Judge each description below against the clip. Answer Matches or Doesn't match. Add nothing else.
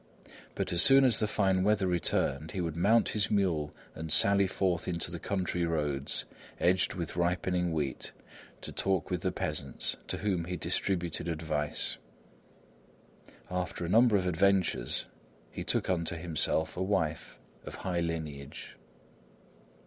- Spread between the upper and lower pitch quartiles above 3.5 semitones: Doesn't match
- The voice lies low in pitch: Matches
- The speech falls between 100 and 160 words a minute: Matches